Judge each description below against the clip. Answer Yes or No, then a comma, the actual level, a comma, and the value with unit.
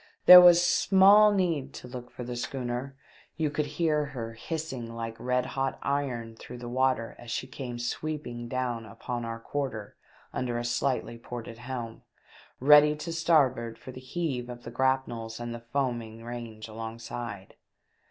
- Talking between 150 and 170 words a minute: Yes, average, 160 wpm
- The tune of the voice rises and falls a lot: No, average, 3.4 semitones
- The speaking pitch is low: Yes, low, 125 Hz